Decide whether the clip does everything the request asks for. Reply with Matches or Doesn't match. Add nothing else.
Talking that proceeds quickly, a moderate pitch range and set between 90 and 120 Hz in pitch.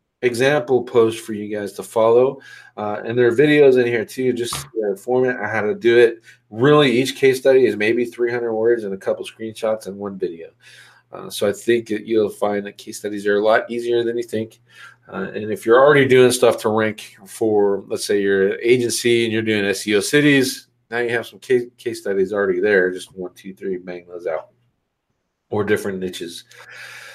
Matches